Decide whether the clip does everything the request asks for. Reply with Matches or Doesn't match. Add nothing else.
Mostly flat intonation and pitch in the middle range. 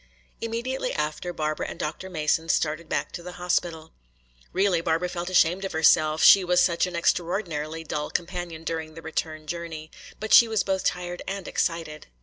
Matches